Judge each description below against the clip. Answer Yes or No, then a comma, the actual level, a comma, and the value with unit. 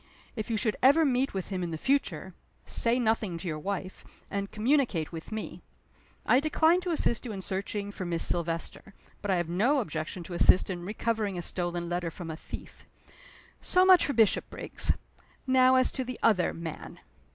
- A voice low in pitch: No, high, 200 Hz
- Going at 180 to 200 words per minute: Yes, average, 185 wpm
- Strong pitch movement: Yes, wide, 6.4 semitones